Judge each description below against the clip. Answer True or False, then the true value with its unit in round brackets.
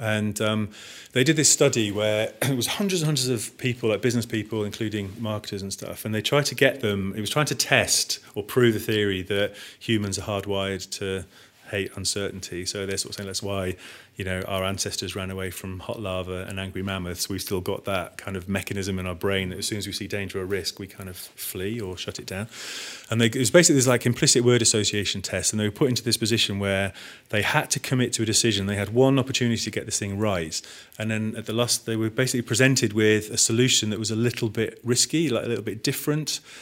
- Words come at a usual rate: False (240 wpm)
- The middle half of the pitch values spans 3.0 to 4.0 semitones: True (3.6 semitones)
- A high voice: False (110 Hz)